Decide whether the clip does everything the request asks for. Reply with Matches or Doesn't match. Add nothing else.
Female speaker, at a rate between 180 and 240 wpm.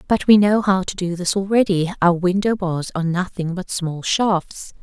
Matches